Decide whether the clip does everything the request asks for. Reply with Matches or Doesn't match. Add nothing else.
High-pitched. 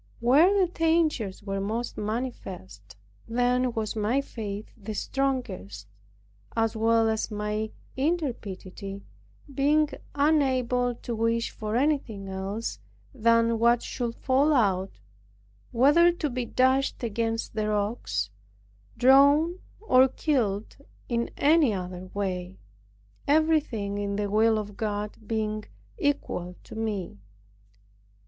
Matches